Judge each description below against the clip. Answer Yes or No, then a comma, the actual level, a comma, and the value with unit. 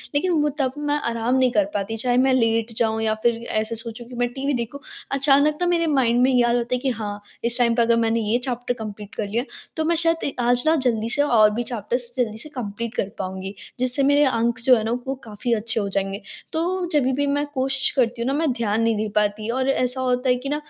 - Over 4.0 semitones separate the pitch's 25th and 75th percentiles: No, average, 3.1 semitones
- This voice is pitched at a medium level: No, high, 240 Hz